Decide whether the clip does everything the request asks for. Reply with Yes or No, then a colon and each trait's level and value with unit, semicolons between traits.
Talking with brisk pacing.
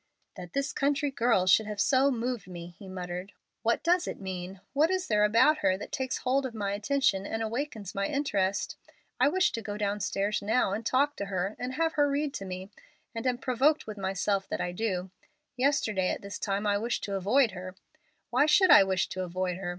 Yes: fast, 210 wpm